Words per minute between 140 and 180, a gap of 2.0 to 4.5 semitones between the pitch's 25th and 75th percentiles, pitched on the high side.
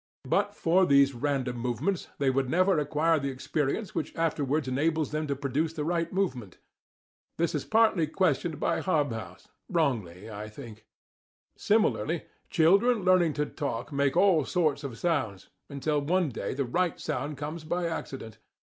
No: average, 155 wpm; average, 4.1 semitones; medium, 150 Hz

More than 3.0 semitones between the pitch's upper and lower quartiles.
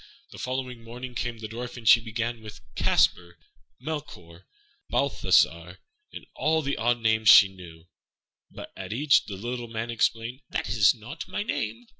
No: narrow, 2.5 semitones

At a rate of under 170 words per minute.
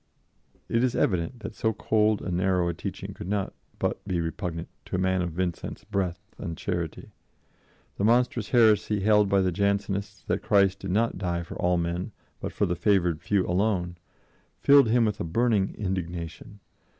No: average, 175 wpm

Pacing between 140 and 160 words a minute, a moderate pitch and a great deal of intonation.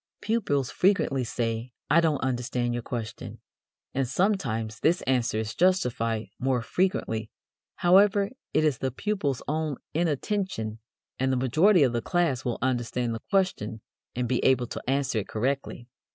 No: average, 150 wpm; low, 130 Hz; wide, 6.2 semitones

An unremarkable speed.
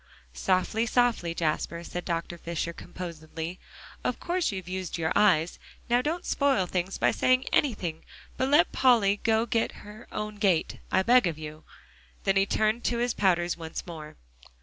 Yes: average, 160 wpm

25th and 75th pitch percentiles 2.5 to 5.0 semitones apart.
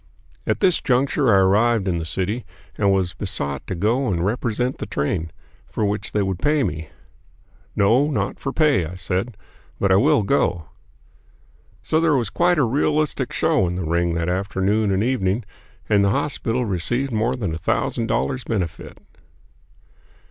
No: wide, 5.4 semitones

